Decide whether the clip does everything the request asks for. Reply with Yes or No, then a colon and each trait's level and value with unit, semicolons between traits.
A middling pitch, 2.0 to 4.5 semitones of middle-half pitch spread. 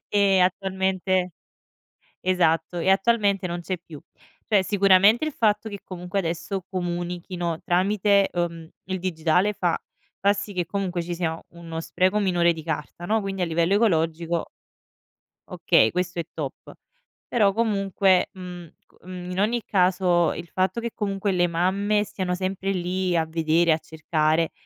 Yes: medium, 180 Hz; narrow, 2.5 semitones